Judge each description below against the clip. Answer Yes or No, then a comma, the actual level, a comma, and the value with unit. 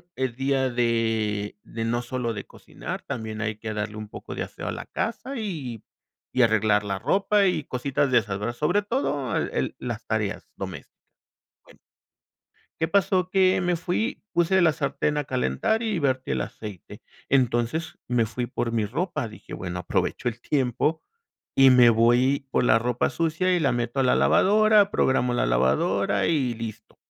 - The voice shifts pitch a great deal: Yes, wide, 6.5 semitones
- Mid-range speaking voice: No, low, 125 Hz